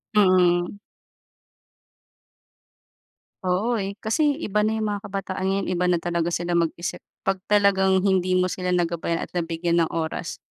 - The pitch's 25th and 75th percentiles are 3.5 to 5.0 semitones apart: No, narrow, 2.5 semitones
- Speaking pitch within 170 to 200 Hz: Yes, medium, 185 Hz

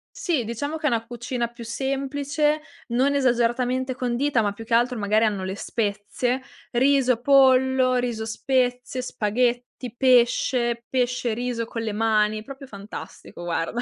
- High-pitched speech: Yes, high, 245 Hz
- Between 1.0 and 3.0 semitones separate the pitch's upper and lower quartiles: Yes, narrow, 2.5 semitones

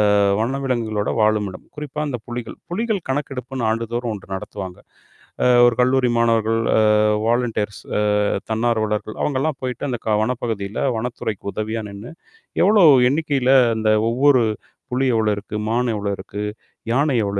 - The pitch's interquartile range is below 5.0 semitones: Yes, average, 3.4 semitones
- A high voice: No, low, 120 Hz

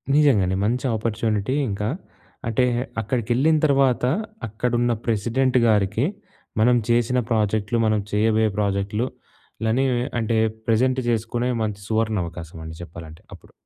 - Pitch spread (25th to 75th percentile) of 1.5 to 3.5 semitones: Yes, average, 3.0 semitones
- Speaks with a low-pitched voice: Yes, low, 110 Hz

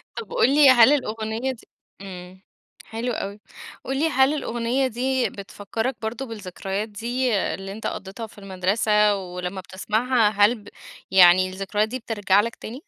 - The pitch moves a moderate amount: Yes, average, 4.2 semitones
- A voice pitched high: Yes, high, 220 Hz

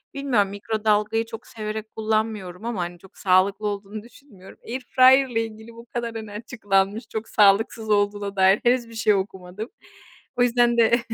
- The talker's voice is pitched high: Yes, high, 215 Hz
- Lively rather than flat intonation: No, narrow, 2.4 semitones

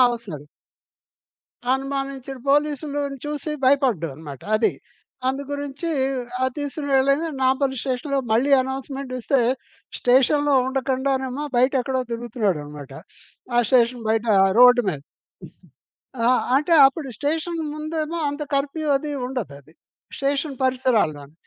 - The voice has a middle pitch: No, very high, 265 Hz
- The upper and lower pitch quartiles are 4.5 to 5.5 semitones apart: No, average, 2.9 semitones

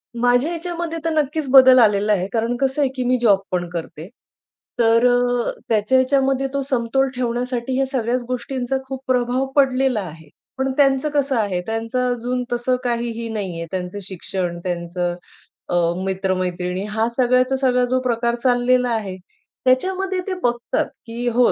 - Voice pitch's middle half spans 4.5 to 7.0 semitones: No, average, 3.6 semitones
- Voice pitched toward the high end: Yes, high, 245 Hz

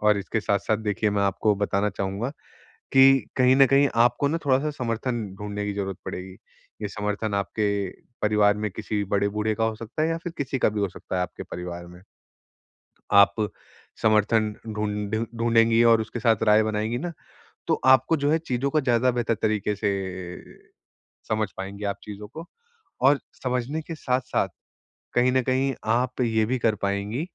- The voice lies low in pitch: Yes, low, 110 Hz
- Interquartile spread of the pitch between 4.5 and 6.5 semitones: No, average, 3.6 semitones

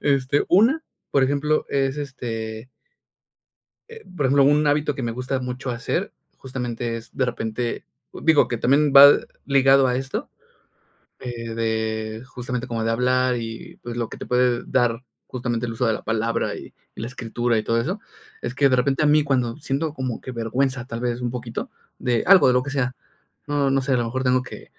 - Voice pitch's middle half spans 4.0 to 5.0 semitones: No, average, 2.8 semitones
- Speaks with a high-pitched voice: No, low, 125 Hz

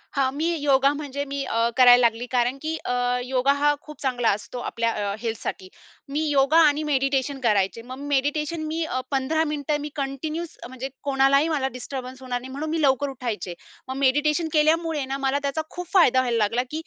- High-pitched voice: Yes, very high, 275 Hz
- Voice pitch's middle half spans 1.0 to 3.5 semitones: Yes, average, 3.0 semitones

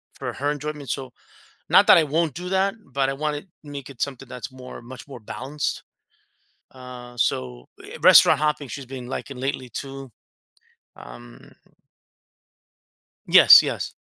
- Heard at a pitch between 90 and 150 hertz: Yes, low, 135 Hz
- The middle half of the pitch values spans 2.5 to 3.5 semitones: Yes, average, 2.9 semitones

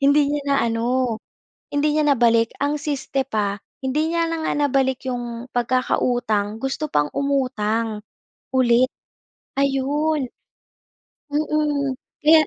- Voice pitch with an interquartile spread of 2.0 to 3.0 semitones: No, average, 3.6 semitones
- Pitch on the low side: No, very high, 265 Hz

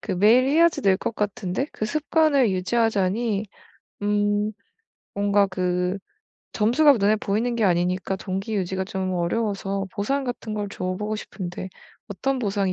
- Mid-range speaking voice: No, high, 205 Hz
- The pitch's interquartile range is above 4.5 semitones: No, average, 3.3 semitones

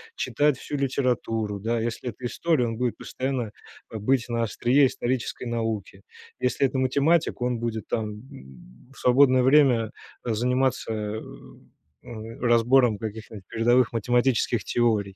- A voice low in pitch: Yes, low, 120 Hz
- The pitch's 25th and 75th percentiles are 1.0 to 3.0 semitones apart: Yes, average, 2.7 semitones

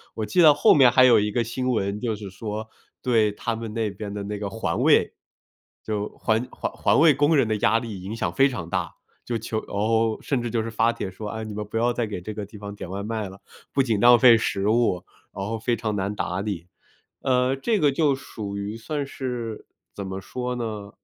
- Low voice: Yes, low, 110 Hz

